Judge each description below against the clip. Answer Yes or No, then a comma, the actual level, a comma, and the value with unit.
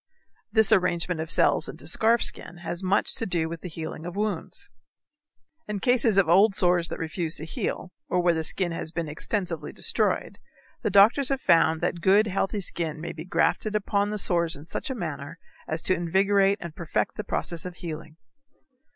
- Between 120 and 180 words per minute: No, average, 190 wpm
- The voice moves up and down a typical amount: Yes, average, 3.5 semitones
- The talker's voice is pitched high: No, medium, 175 Hz